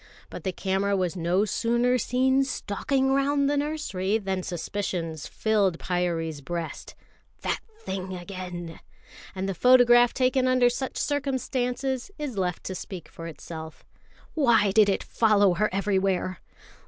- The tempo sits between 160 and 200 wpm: No, average, 140 wpm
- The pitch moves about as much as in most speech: No, wide, 5.7 semitones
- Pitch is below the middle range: No, high, 200 Hz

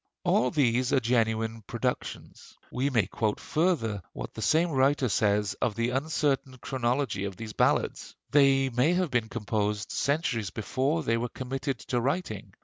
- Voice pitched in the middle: No, low, 125 Hz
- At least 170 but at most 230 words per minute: No, average, 155 wpm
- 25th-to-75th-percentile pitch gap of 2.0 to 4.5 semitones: Yes, average, 3.7 semitones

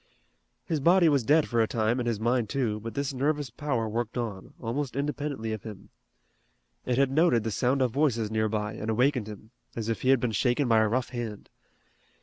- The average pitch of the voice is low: Yes, low, 120 Hz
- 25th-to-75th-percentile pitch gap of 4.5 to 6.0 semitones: No, average, 3.8 semitones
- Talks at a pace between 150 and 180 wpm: No, fast, 205 wpm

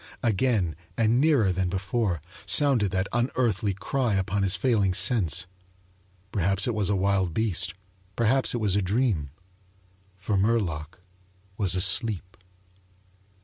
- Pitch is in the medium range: No, low, 100 Hz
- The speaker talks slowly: Yes, slow, 125 wpm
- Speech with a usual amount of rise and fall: Yes, average, 3.8 semitones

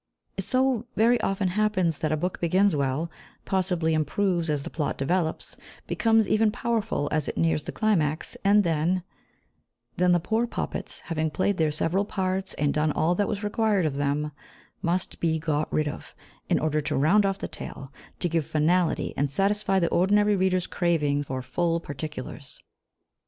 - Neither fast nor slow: Yes, average, 175 wpm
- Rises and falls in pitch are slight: No, average, 4.5 semitones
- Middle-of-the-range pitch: Yes, medium, 170 Hz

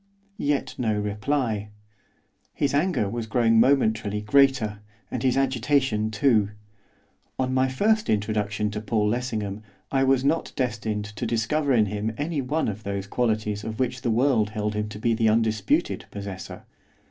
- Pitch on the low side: Yes, low, 110 Hz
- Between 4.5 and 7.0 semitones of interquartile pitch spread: No, average, 3.7 semitones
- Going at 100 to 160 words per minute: Yes, average, 155 wpm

